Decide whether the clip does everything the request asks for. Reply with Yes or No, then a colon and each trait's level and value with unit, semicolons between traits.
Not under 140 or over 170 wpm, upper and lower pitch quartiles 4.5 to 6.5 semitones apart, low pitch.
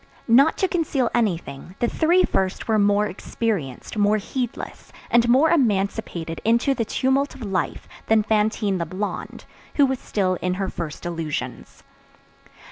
No: average, 145 wpm; average, 5.1 semitones; high, 210 Hz